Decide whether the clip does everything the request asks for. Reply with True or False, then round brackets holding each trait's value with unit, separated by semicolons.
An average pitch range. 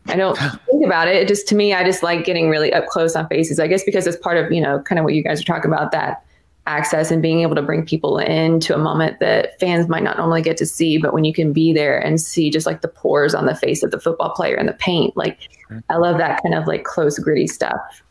False (1.5 semitones)